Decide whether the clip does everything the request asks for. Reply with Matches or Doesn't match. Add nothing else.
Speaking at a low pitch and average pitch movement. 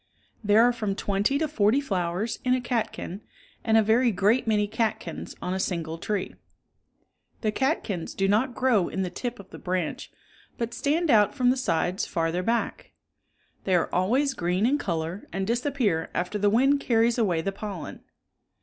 Doesn't match